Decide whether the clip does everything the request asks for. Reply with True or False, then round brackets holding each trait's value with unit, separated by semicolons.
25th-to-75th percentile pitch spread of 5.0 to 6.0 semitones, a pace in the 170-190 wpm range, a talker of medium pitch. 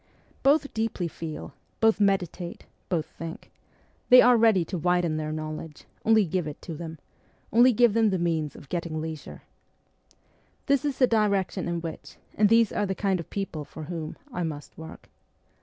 True (5.4 semitones; 175 wpm; 180 Hz)